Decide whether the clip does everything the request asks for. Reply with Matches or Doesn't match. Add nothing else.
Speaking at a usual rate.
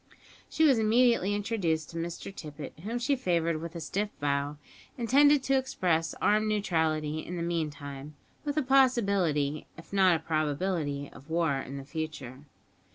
Matches